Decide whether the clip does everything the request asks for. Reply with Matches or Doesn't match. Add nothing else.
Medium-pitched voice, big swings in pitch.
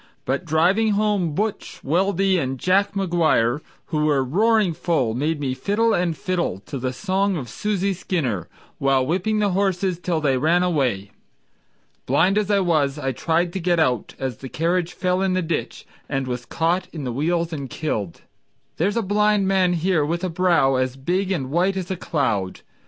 Matches